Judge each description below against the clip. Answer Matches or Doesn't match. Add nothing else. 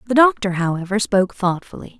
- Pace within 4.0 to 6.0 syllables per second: Doesn't match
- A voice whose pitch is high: Matches